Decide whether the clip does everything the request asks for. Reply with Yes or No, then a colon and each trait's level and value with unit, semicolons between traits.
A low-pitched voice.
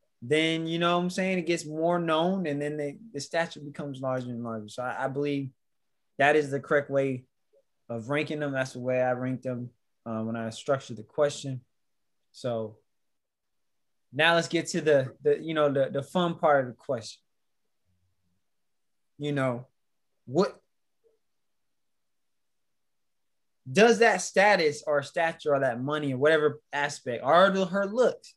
No: medium, 145 Hz